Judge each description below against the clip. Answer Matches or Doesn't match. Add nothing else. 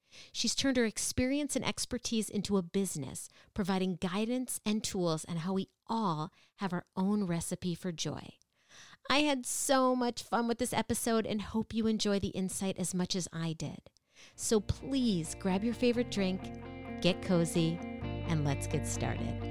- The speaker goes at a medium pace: Matches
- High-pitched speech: Matches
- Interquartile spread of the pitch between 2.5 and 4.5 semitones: Doesn't match